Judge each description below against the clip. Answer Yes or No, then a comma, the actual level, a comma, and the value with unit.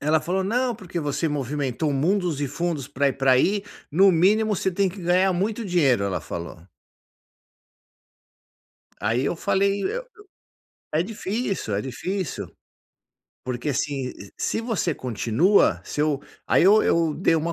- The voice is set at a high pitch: No, medium, 165 Hz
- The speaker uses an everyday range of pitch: No, wide, 6.0 semitones